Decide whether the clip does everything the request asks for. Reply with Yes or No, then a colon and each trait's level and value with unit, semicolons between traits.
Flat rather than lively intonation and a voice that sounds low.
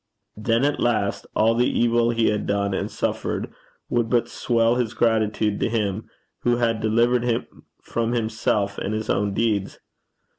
Yes: narrow, 1.9 semitones; low, 115 Hz